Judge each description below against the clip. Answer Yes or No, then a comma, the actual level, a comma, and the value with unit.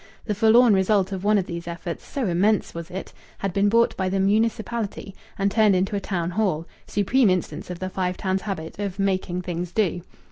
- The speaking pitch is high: Yes, high, 195 Hz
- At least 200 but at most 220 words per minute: Yes, fast, 205 wpm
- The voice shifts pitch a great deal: No, narrow, 2.6 semitones